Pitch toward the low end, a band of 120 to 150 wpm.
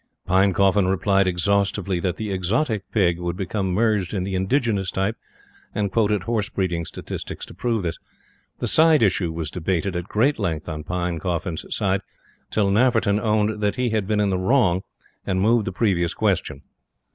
No: very low, 95 Hz; average, 170 wpm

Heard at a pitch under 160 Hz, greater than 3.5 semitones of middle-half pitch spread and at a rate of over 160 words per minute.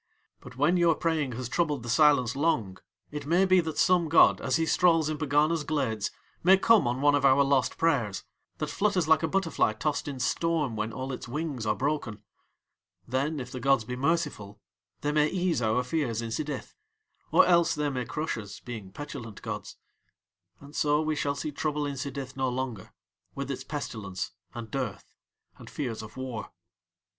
Yes: medium, 140 Hz; average, 4.1 semitones; average, 185 wpm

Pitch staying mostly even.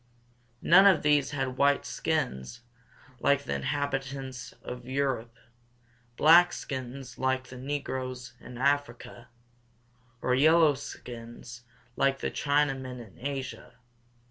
Yes: narrow, 2.2 semitones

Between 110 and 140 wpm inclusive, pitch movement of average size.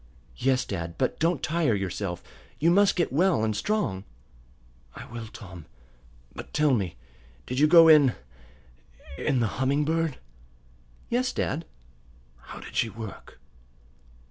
No: slow, 135 wpm; wide, 7.4 semitones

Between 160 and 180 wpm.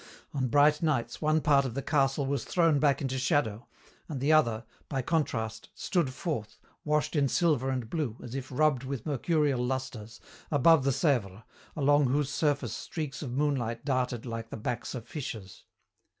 Yes: average, 170 wpm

